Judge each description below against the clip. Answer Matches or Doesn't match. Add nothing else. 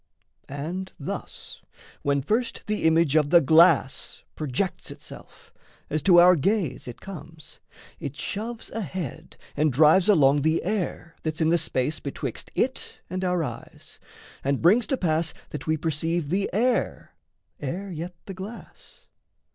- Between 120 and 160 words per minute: Matches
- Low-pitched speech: Doesn't match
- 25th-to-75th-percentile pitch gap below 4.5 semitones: Matches